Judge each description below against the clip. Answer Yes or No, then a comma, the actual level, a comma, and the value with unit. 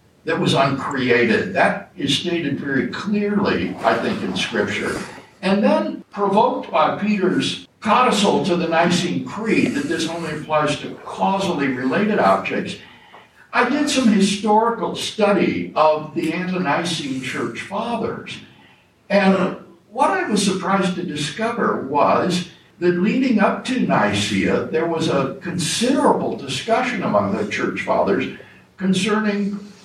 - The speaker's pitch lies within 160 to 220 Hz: Yes, high, 190 Hz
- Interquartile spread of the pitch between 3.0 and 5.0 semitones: Yes, average, 4.4 semitones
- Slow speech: Yes, slow, 125 wpm